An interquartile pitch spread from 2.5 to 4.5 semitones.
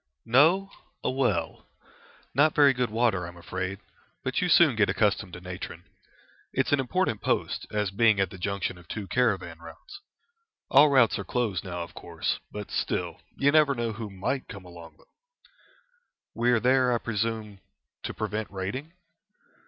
No: average, 5.3 semitones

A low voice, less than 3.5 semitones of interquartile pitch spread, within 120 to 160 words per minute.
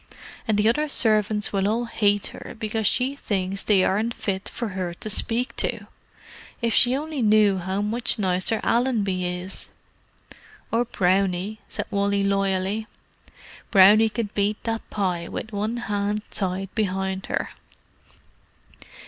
No: high, 205 Hz; average, 2.7 semitones; average, 140 wpm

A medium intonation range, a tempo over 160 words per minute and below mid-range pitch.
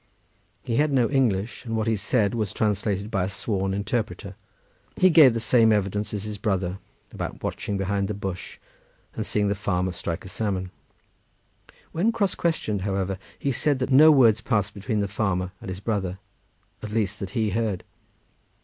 Yes: average, 3.1 semitones; average, 175 wpm; low, 105 Hz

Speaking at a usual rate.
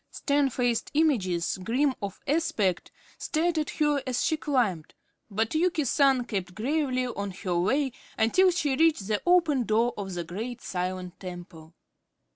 Yes: average, 150 wpm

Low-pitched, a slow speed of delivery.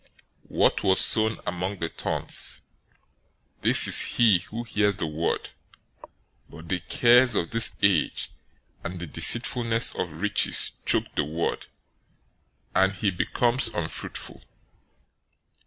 Yes: very low, 95 Hz; slow, 125 wpm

